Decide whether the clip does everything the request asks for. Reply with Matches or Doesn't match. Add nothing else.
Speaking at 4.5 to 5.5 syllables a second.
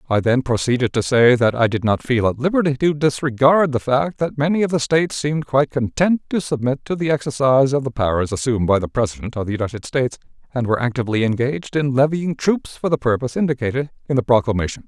Doesn't match